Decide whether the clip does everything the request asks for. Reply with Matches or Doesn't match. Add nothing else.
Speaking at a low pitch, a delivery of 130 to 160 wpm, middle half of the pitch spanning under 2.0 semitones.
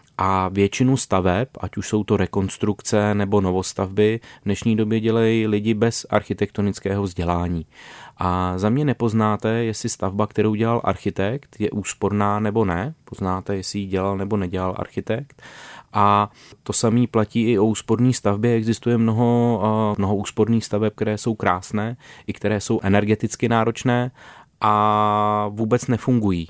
Doesn't match